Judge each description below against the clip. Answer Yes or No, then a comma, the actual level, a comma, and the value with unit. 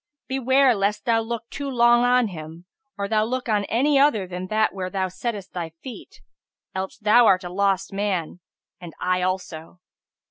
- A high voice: Yes, high, 205 Hz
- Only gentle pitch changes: No, average, 4.5 semitones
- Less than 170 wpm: No, average, 175 wpm